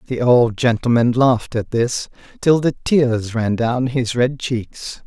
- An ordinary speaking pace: Yes, average, 165 wpm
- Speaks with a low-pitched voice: Yes, low, 120 Hz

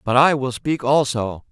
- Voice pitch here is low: Yes, low, 130 Hz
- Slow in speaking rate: No, average, 200 wpm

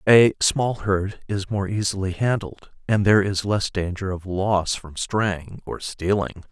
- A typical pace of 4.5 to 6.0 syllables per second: No, 4.0 syllables/s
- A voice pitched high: No, low, 100 Hz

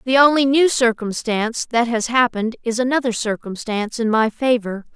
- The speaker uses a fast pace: No, average, 160 wpm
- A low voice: No, high, 235 Hz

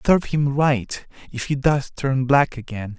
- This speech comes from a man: Yes, male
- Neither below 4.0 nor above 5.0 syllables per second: Yes, 4.2 syllables/s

